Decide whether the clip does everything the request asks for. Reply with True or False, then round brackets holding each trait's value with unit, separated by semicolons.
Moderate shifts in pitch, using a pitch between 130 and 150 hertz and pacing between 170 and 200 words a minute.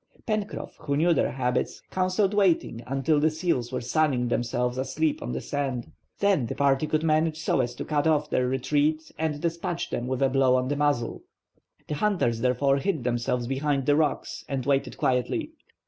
True (3.8 semitones; 140 Hz; 185 wpm)